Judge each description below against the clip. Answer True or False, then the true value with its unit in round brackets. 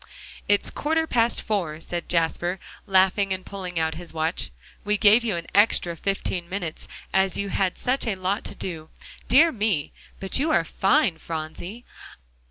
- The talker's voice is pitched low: False (190 Hz)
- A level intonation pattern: False (3.7 semitones)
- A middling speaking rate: True (165 wpm)